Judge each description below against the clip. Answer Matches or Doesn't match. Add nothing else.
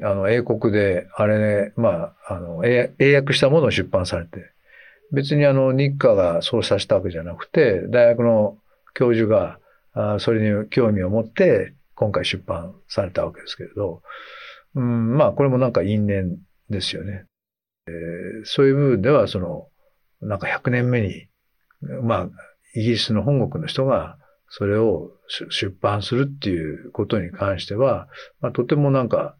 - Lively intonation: Doesn't match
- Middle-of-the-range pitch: Doesn't match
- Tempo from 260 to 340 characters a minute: Matches